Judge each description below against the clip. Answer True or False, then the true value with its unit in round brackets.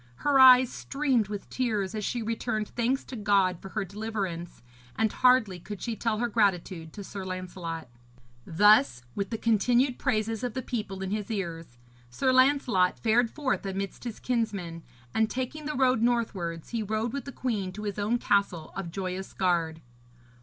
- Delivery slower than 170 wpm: False (175 wpm)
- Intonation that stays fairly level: False (4.3 semitones)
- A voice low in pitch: False (215 Hz)